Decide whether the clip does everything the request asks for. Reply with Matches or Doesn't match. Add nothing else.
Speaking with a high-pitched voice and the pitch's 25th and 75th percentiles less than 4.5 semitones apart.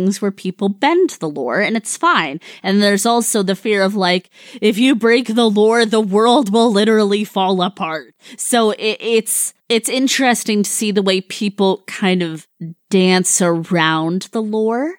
Matches